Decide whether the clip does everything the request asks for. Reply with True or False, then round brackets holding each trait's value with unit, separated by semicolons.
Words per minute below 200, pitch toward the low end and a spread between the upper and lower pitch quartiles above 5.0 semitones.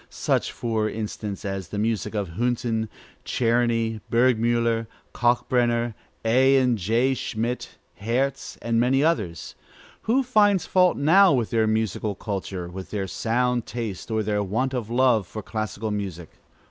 False (140 wpm; 115 Hz; 2.7 semitones)